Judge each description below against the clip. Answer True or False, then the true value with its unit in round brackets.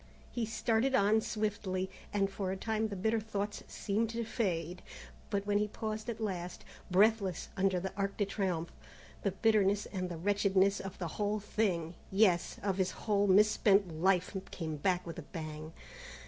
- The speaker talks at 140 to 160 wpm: False (170 wpm)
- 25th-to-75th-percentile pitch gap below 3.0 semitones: True (2.6 semitones)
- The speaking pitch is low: False (200 Hz)